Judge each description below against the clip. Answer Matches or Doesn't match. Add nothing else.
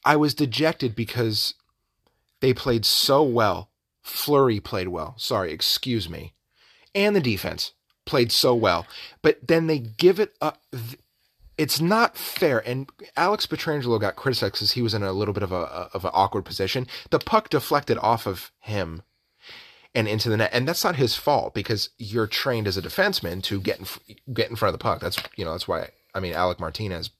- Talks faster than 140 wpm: Matches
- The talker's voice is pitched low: Matches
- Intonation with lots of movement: Matches